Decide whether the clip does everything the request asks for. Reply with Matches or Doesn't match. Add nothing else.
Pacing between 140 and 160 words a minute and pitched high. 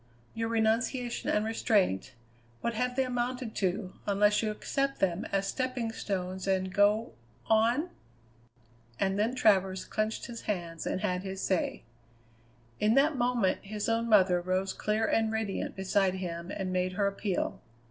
Matches